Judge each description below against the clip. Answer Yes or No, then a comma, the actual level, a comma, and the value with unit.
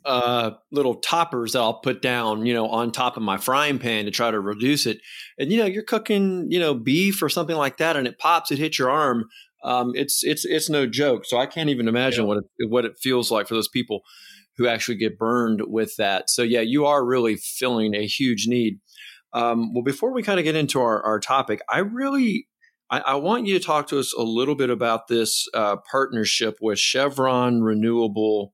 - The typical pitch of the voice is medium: No, low, 125 Hz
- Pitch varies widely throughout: No, average, 4.7 semitones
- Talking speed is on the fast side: Yes, fast, 220 wpm